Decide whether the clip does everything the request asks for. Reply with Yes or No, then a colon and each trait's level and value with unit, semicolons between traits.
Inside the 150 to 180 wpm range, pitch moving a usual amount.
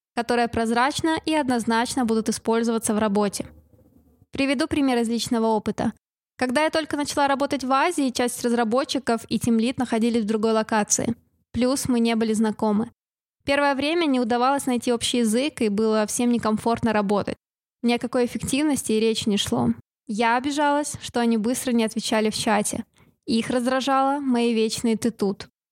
Yes: average, 155 wpm; average, 3.0 semitones